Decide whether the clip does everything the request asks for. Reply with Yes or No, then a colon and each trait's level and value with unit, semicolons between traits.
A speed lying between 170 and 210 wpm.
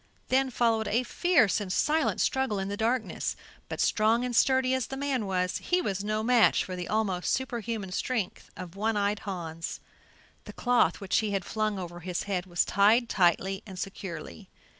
Yes: average, 185 wpm